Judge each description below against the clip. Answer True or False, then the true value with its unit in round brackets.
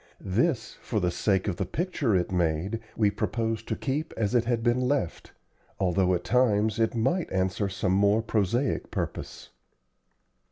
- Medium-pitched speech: False (110 Hz)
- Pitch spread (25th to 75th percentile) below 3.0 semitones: False (4.3 semitones)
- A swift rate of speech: False (160 wpm)